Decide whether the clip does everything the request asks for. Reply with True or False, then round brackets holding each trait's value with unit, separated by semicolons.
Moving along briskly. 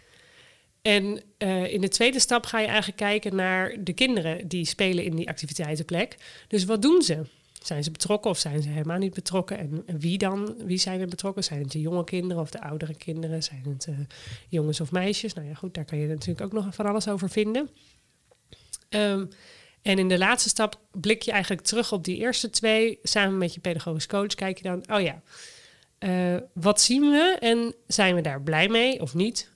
True (210 wpm)